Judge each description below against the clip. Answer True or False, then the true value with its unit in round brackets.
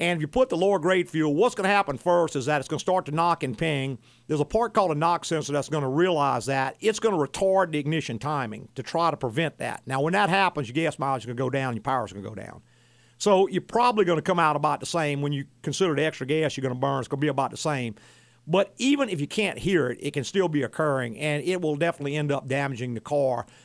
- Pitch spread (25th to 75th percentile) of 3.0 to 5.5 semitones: True (4.7 semitones)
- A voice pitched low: False (150 Hz)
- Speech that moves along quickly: True (290 wpm)